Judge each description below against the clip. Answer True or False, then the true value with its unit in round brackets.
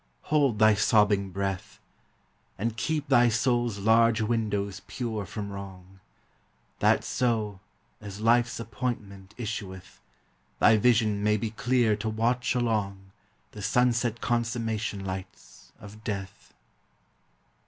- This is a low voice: True (110 Hz)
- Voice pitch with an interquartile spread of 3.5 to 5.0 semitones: False (2.7 semitones)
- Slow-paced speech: True (110 wpm)